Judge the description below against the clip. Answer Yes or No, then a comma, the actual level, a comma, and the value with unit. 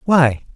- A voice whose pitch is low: No, medium, 145 Hz